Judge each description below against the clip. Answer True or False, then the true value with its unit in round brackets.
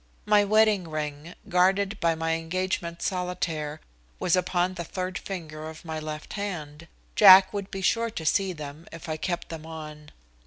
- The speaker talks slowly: False (165 wpm)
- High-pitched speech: False (170 Hz)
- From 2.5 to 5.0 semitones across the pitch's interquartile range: True (3.2 semitones)